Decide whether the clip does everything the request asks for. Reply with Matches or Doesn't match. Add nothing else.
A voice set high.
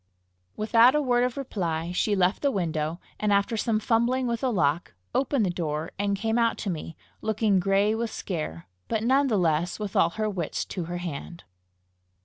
Matches